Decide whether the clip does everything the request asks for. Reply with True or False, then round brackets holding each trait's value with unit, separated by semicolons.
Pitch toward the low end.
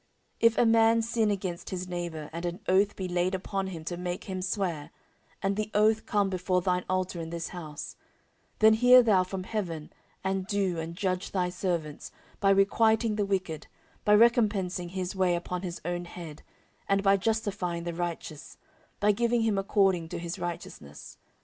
False (185 Hz)